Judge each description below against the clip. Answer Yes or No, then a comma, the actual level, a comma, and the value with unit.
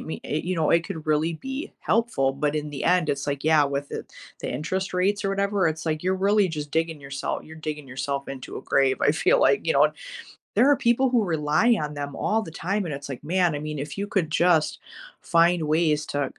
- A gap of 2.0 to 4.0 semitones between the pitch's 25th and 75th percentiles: No, average, 4.4 semitones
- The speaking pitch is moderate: Yes, medium, 160 Hz